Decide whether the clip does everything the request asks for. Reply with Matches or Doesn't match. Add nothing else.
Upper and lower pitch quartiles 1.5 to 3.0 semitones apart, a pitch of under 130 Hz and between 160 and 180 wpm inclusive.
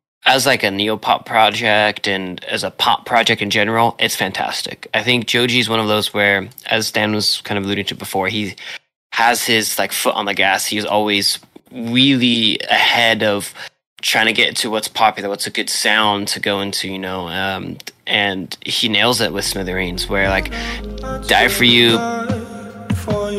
Matches